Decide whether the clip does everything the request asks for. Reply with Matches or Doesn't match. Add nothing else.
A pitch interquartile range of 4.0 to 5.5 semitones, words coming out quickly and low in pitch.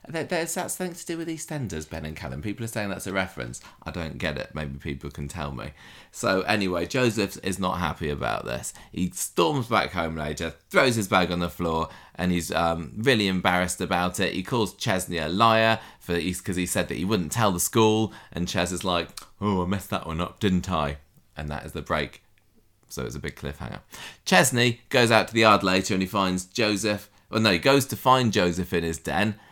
Matches